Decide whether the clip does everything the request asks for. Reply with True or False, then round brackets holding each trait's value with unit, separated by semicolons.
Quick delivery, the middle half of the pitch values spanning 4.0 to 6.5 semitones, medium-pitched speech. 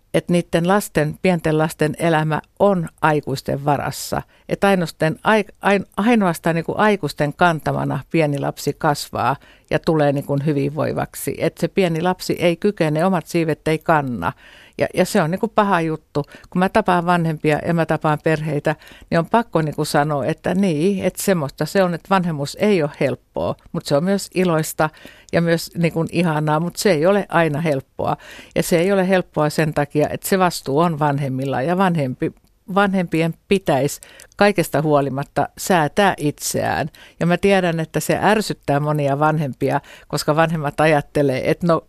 False (160 wpm; 3.5 semitones; 160 Hz)